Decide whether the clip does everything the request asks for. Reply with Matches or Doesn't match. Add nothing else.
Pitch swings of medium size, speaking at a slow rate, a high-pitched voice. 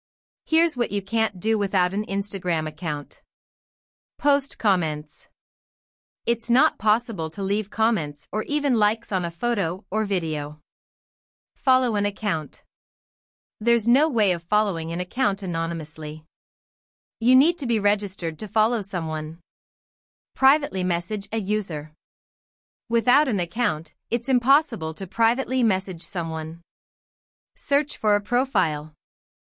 Doesn't match